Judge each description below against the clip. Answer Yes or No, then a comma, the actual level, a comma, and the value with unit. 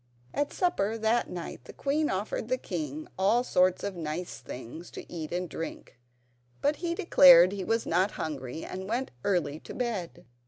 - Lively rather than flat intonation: Yes, wide, 6.5 semitones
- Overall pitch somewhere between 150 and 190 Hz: Yes, medium, 185 Hz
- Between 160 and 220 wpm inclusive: Yes, average, 170 wpm